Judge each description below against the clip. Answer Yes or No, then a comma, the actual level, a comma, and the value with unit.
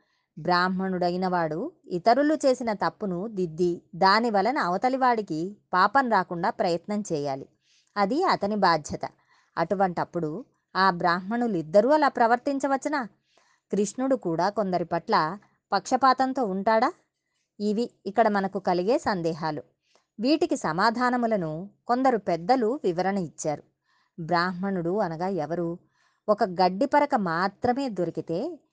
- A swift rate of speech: No, average, 95 wpm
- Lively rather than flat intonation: Yes, wide, 5.8 semitones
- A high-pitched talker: Yes, high, 200 Hz